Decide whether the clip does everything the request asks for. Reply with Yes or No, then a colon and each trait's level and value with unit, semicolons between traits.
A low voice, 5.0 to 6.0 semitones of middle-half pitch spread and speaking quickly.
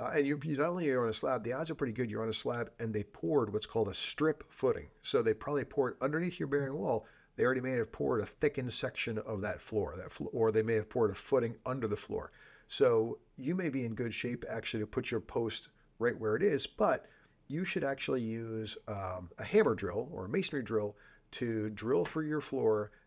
Yes: low, 125 Hz; wide, 5.5 semitones; fast, 240 wpm